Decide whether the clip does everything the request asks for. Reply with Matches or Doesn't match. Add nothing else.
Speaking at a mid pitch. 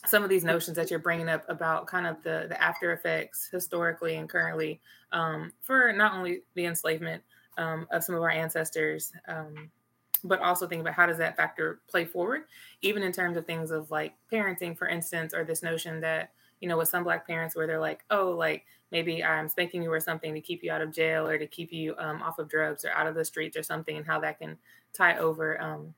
Matches